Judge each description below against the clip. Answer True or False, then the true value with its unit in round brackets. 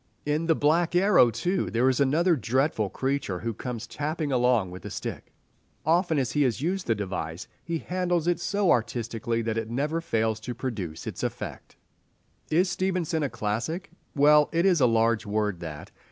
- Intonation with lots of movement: True (6.7 semitones)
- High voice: False (135 Hz)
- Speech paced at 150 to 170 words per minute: False (180 wpm)